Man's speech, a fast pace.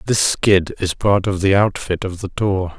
Yes: male; fast, 215 wpm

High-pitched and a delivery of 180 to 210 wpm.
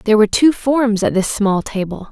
No: high, 220 Hz; fast, 225 wpm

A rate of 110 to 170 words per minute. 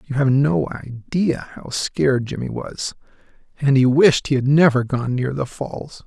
No: average, 180 wpm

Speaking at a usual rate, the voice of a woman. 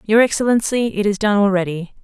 Yes: average, 175 wpm; female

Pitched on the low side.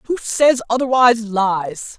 No: high, 230 Hz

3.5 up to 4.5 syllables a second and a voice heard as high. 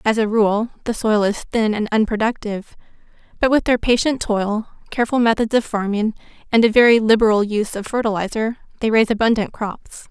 No: 5.8 syllables/s; high, 220 Hz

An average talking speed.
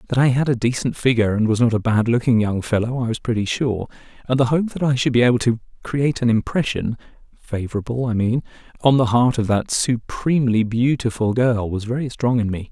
No: fast, 215 wpm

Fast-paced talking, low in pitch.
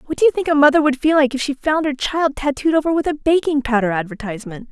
No: fast, 265 wpm; very high, 280 Hz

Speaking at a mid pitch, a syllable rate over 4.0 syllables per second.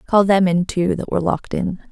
Yes: medium, 180 Hz; 6.1 syllables/s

